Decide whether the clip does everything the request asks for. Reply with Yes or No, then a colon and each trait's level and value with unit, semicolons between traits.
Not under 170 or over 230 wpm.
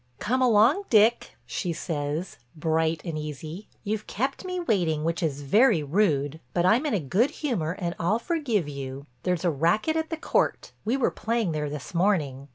Yes: average, 175 wpm